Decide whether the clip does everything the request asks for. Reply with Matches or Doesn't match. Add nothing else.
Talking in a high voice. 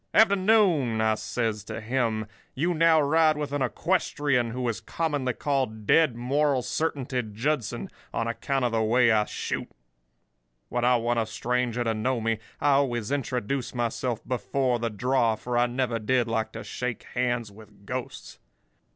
Doesn't match